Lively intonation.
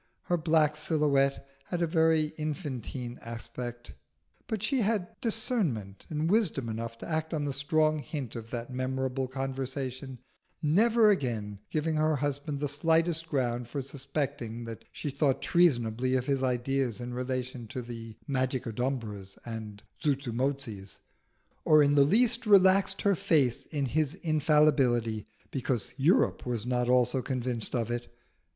No: average, 4.3 semitones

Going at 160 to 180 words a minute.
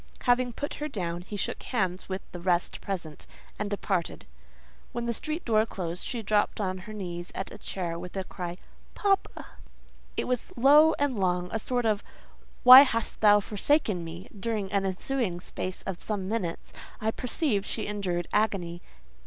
Yes: average, 170 wpm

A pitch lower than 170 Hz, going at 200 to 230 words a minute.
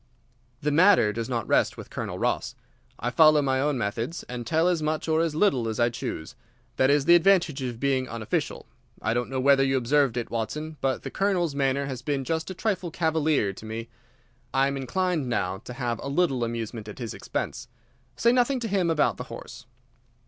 Yes: low, 135 Hz; fast, 205 wpm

